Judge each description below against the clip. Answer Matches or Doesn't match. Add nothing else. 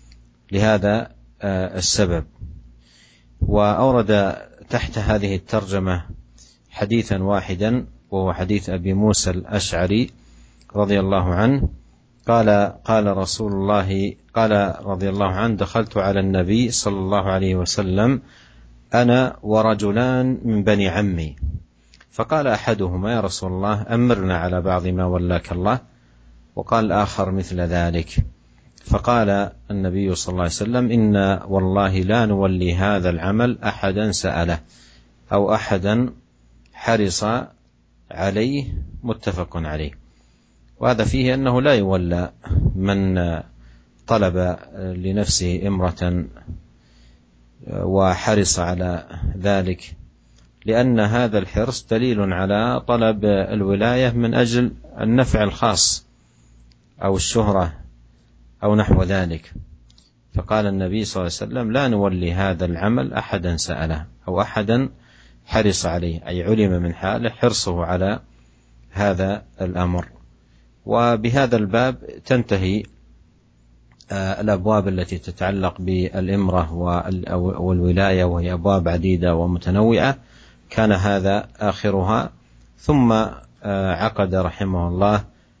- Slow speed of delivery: Doesn't match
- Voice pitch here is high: Doesn't match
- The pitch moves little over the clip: Doesn't match